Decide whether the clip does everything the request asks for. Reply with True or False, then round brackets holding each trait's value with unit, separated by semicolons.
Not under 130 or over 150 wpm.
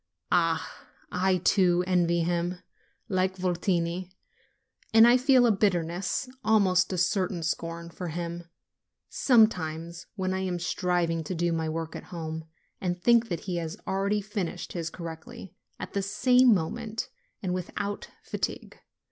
True (140 wpm)